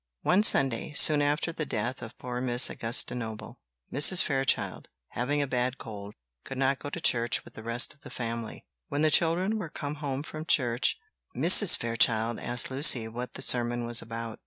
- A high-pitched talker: No, low, 125 Hz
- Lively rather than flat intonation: No, average, 3.8 semitones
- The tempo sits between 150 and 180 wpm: No, average, 190 wpm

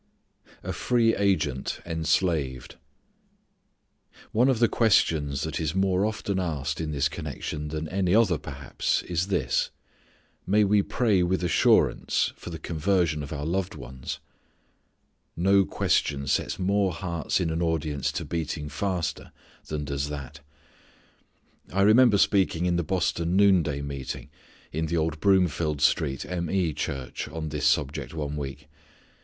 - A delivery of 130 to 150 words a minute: Yes, average, 140 wpm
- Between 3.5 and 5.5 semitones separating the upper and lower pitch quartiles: Yes, average, 4.4 semitones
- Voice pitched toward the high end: No, very low, 80 Hz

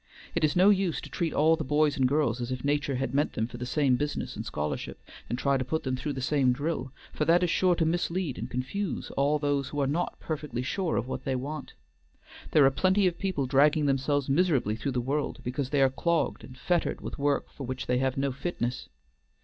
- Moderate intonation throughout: Yes, average, 3.5 semitones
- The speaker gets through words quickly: Yes, fast, 235 wpm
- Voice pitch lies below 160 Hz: Yes, medium, 140 Hz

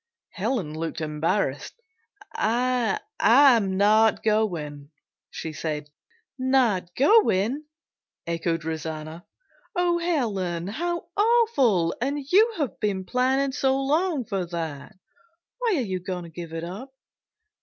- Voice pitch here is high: Yes, high, 210 Hz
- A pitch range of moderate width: No, wide, 8.2 semitones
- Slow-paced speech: Yes, slow, 115 wpm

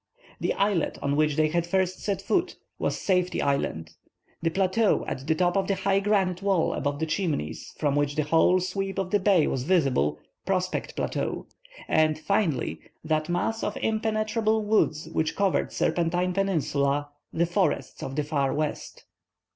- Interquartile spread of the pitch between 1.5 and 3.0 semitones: No, average, 4.3 semitones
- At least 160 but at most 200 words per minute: Yes, average, 165 wpm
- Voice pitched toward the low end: No, medium, 175 Hz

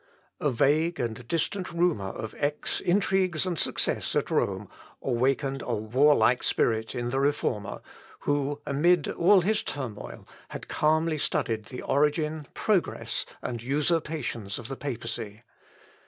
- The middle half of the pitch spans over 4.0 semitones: Yes, average, 5.2 semitones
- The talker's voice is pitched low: No, medium, 145 Hz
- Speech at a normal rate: No, slow, 130 wpm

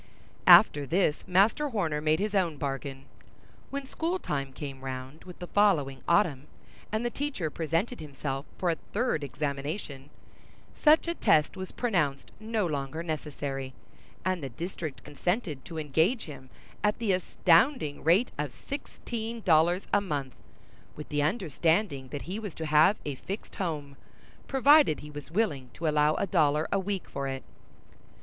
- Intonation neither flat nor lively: No, wide, 5.9 semitones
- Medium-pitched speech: Yes, medium, 160 Hz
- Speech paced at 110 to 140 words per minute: No, average, 155 wpm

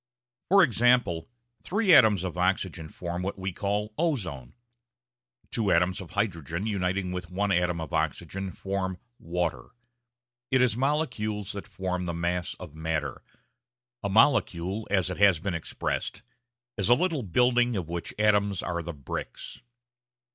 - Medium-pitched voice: No, very low, 95 Hz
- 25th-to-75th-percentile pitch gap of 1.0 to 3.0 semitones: No, average, 3.7 semitones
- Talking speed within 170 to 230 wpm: No, average, 145 wpm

